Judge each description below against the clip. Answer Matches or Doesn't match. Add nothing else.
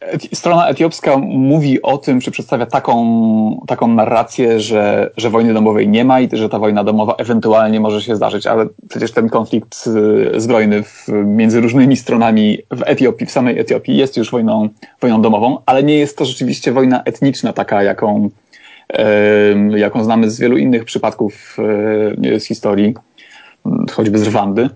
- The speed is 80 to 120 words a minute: Doesn't match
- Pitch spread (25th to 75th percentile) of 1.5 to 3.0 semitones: Matches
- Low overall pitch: Matches